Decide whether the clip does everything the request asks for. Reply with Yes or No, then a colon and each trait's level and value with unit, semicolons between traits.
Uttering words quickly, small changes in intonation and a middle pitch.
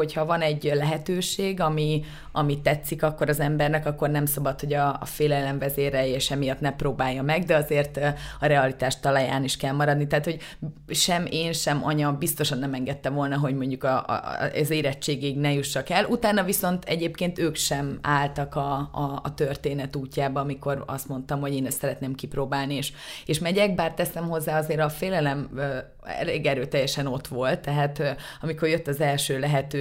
Yes: fast, 190 wpm; narrow, 2.0 semitones; medium, 145 Hz